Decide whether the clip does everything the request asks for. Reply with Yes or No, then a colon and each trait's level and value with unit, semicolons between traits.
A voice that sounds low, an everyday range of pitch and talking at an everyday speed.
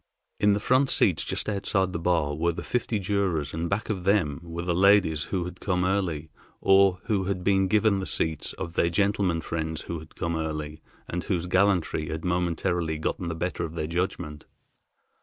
Yes: very low, 90 Hz; average, 3.3 semitones; average, 195 wpm